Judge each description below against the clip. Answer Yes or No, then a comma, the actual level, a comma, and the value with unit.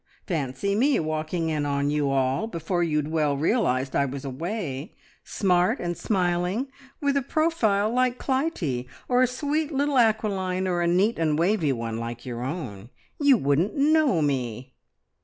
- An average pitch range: No, wide, 8.3 semitones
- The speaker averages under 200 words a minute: Yes, average, 160 wpm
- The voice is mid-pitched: Yes, medium, 175 Hz